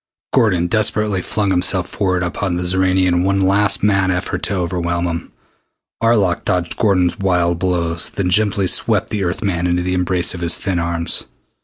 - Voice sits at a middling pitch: No, very low, 90 Hz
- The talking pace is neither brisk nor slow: Yes, average, 175 wpm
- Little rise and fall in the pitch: Yes, narrow, 2.0 semitones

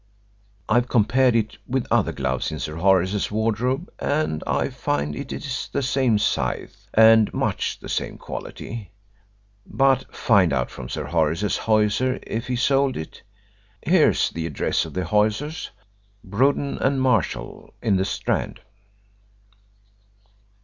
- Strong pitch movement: Yes, wide, 5.8 semitones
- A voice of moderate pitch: No, low, 110 Hz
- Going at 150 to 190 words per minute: No, slow, 135 wpm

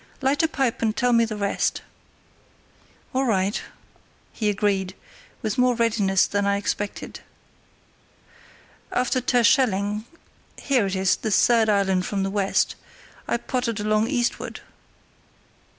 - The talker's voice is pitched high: Yes, high, 215 Hz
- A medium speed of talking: No, slow, 120 wpm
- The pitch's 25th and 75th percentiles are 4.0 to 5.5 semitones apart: No, average, 3.4 semitones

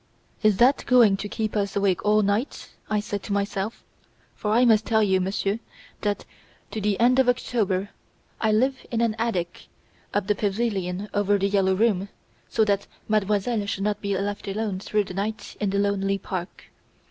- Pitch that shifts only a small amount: Yes, narrow, 1.9 semitones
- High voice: Yes, high, 205 Hz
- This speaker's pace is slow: No, average, 180 wpm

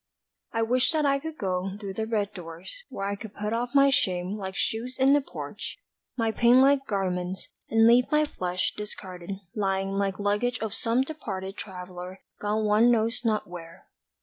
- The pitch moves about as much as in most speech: Yes, average, 4.3 semitones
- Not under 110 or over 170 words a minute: No, average, 180 wpm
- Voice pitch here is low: No, high, 210 Hz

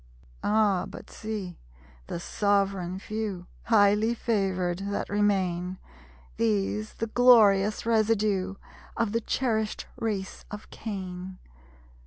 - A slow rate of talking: Yes, slow, 100 wpm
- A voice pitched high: Yes, high, 200 Hz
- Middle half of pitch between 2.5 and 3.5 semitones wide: Yes, average, 2.8 semitones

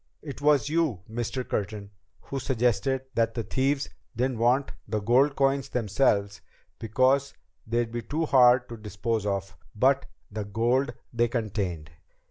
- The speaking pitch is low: Yes, low, 120 Hz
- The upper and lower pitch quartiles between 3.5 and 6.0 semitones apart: Yes, average, 4.0 semitones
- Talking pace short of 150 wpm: Yes, average, 140 wpm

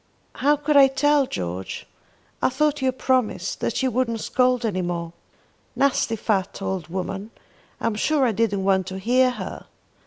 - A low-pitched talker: No, high, 230 Hz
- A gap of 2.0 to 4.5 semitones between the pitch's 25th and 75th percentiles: No, wide, 5.6 semitones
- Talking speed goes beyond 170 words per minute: No, average, 165 wpm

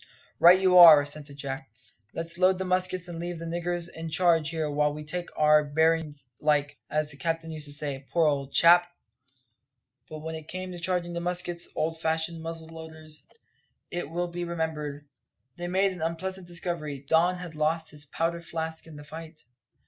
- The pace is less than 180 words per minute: No, average, 185 wpm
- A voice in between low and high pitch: Yes, medium, 165 Hz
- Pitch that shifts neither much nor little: No, narrow, 2.3 semitones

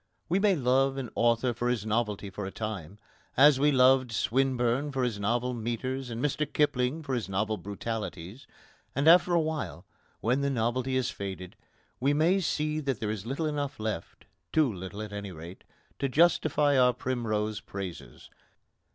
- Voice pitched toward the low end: Yes, low, 125 Hz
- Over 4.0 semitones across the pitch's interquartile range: Yes, average, 4.5 semitones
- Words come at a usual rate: Yes, average, 170 wpm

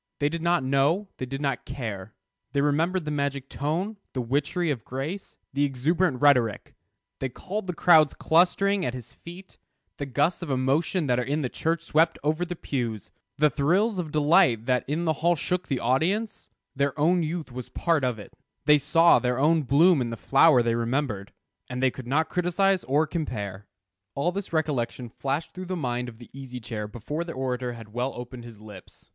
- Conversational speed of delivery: Yes, average, 195 wpm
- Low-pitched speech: No, medium, 145 Hz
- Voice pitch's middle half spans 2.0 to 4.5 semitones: No, average, 5.0 semitones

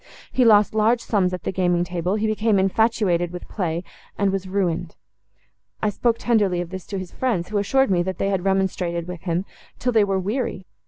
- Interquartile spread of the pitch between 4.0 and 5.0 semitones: No, average, 3.2 semitones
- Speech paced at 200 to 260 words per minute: Yes, fast, 205 wpm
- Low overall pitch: No, high, 190 Hz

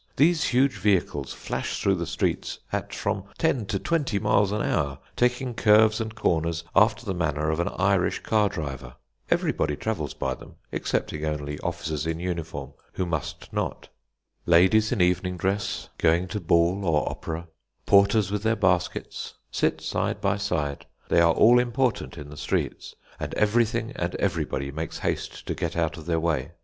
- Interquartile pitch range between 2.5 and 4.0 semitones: No, average, 5.0 semitones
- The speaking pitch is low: Yes, very low, 90 Hz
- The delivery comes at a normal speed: Yes, average, 170 wpm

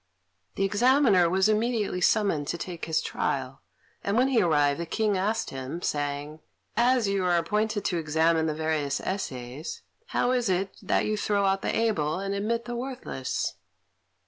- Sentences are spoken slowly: No, average, 170 wpm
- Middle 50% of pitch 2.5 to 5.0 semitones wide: No, wide, 5.5 semitones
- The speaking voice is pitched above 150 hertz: Yes, high, 190 Hz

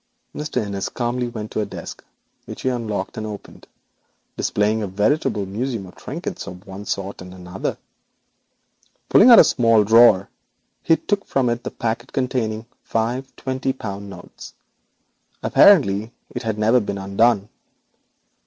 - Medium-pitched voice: No, low, 110 Hz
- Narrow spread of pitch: No, average, 3.8 semitones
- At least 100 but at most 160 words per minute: Yes, average, 150 wpm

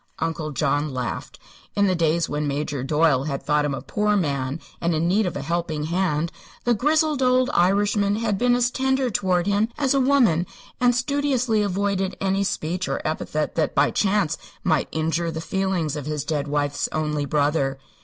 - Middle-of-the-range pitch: Yes, medium, 170 Hz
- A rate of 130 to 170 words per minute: No, average, 185 wpm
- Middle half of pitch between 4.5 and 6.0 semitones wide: Yes, wide, 5.6 semitones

